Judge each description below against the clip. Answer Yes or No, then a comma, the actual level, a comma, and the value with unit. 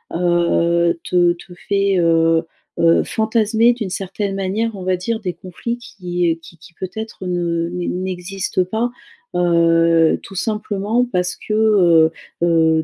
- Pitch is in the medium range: Yes, medium, 180 Hz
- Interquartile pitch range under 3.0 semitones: No, average, 3.4 semitones